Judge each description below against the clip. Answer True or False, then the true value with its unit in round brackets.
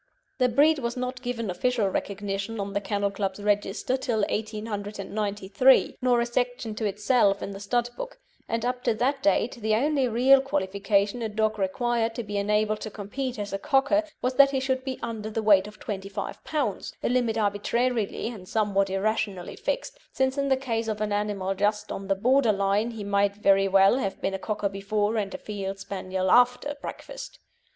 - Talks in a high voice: True (215 Hz)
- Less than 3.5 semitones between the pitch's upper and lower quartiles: False (3.8 semitones)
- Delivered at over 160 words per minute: True (190 wpm)